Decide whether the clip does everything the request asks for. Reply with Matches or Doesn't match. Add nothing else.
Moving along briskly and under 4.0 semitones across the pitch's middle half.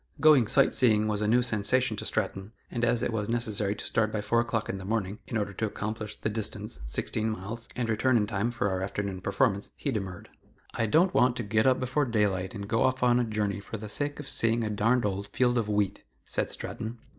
Matches